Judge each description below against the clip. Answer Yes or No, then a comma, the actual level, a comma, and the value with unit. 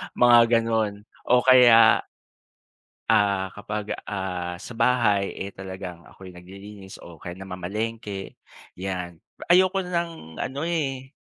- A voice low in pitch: Yes, low, 105 Hz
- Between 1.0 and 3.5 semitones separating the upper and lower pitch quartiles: No, average, 4.4 semitones